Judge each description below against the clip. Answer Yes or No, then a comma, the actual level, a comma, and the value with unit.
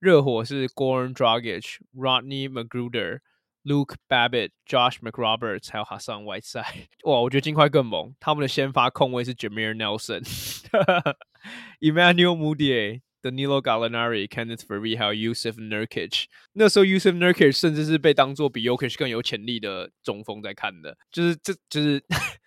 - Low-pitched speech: Yes, low, 130 Hz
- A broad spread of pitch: No, average, 4.8 semitones